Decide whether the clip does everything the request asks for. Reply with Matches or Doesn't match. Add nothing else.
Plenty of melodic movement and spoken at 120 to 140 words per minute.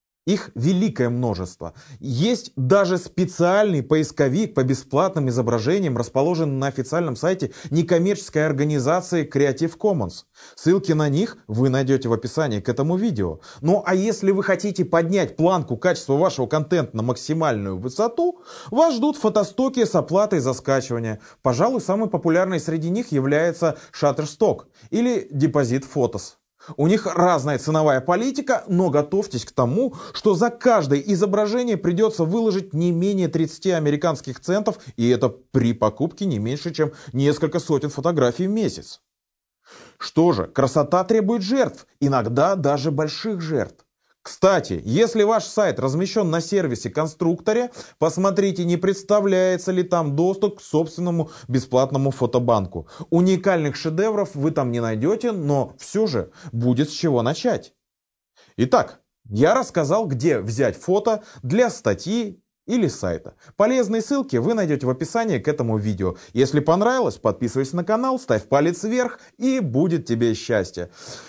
Matches